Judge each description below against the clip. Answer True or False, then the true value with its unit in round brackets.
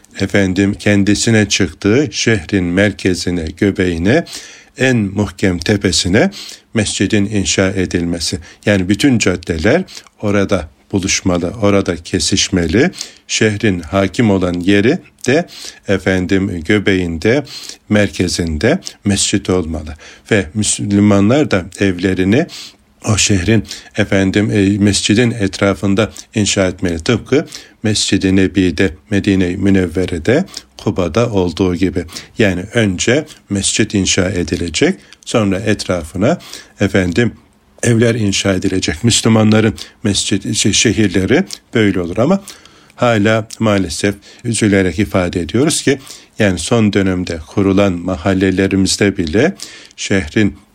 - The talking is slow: True (90 wpm)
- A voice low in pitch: True (100 Hz)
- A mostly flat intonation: True (2.3 semitones)